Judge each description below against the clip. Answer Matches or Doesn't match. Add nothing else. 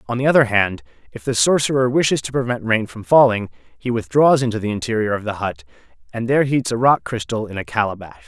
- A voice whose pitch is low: Matches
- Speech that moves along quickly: Matches